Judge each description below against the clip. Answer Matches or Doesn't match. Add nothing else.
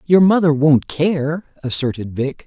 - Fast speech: Doesn't match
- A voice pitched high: Doesn't match